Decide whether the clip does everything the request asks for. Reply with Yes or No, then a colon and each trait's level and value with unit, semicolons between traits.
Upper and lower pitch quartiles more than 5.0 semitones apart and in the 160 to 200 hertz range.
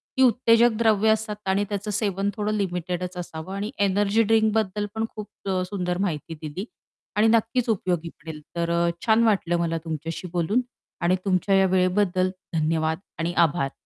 No: average, 3.8 semitones; high, 190 Hz